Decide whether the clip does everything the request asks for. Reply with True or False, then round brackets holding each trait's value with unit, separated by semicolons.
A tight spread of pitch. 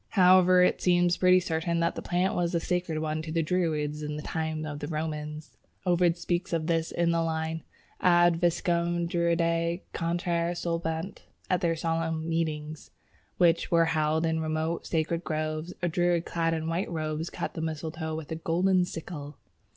True (1.6 semitones)